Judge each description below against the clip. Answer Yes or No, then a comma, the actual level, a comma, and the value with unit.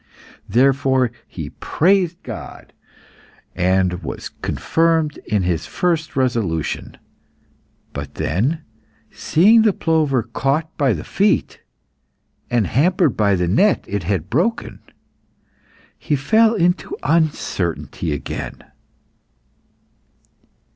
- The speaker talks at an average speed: No, slow, 95 wpm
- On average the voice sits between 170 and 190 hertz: No, low, 135 Hz